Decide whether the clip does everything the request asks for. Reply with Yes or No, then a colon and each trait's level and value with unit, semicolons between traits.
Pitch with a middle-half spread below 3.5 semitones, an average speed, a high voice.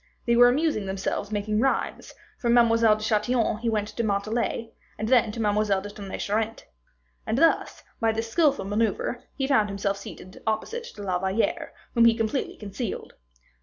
Yes: narrow, 2.4 semitones; average, 170 wpm; high, 220 Hz